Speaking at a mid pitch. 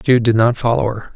No: low, 115 Hz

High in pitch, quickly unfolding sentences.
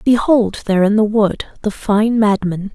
No: high, 210 Hz; average, 175 wpm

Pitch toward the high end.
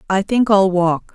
Yes: high, 195 Hz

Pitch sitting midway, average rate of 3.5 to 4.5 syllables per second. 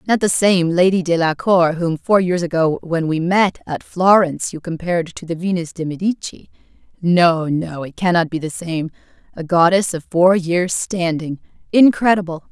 No: medium, 175 Hz; 4.7 syllables/s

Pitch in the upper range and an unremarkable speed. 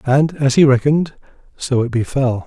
No: low, 135 Hz; average, 170 wpm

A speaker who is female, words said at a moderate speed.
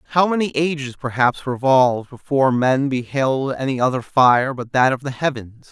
No: male; average, 170 wpm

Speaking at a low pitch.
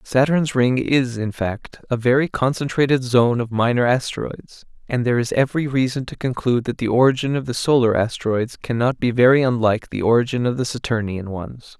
Yes: low, 125 Hz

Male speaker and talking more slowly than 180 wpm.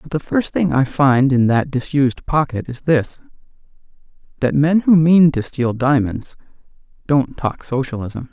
Yes: male; average, 160 wpm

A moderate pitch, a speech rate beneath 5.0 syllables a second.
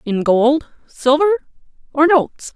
No: very high, 285 Hz; 4.3 syllables/s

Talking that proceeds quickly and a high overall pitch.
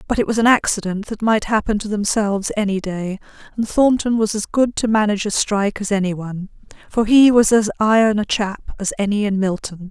Yes: fast, 210 wpm; high, 210 Hz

